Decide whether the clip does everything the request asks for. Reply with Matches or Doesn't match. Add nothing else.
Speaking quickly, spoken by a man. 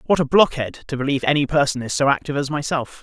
Matches